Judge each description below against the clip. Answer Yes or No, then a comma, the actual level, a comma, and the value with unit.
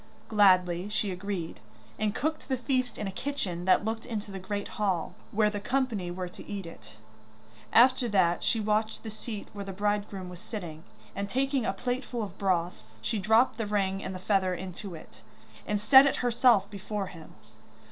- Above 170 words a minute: Yes, average, 190 wpm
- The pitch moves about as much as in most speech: Yes, average, 3.2 semitones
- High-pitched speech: Yes, high, 205 Hz